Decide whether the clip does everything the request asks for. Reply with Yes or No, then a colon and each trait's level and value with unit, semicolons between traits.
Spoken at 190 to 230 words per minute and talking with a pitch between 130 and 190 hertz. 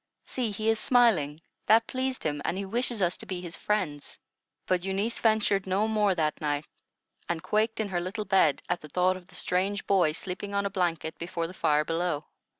Yes: fast, 205 wpm; medium, 185 Hz